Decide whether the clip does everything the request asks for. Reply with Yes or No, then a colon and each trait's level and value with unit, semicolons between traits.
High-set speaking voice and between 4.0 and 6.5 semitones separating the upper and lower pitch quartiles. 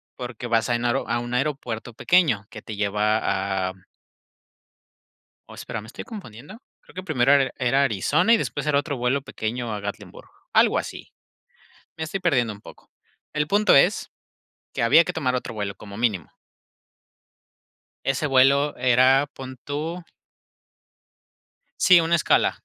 No: low, 125 Hz; average, 4.9 semitones